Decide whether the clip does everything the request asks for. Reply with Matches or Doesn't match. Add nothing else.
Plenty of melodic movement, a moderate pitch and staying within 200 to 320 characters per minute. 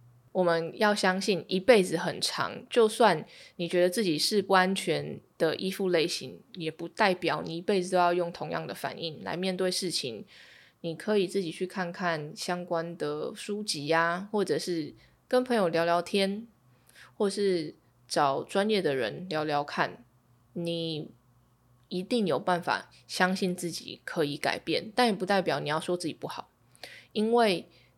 Doesn't match